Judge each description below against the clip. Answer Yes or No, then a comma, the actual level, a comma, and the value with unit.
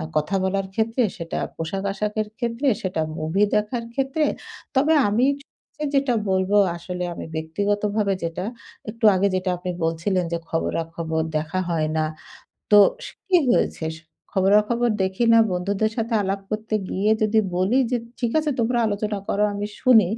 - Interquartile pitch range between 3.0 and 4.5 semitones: Yes, average, 3.9 semitones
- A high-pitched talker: Yes, high, 200 Hz